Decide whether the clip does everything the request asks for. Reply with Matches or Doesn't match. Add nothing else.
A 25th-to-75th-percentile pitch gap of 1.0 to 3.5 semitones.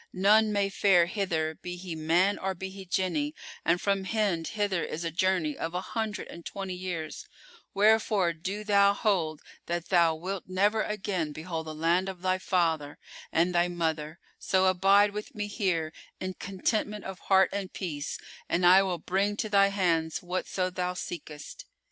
Matches